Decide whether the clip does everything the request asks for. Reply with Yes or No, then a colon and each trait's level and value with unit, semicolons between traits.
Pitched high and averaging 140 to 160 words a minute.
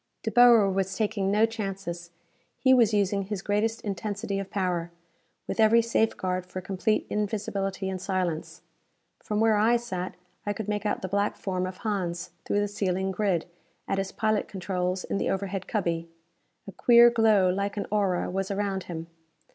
No: high, 200 Hz; average, 170 wpm